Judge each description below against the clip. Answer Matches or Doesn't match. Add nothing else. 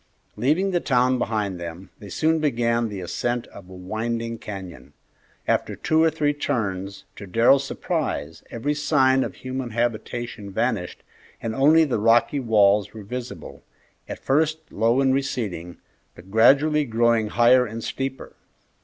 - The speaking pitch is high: Doesn't match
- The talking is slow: Doesn't match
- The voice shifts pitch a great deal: Doesn't match